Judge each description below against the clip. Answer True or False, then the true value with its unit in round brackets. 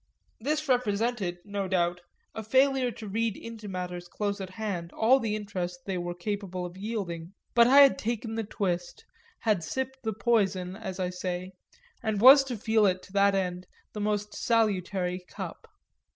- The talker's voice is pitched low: False (205 Hz)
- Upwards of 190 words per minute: False (170 wpm)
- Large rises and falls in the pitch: False (3.8 semitones)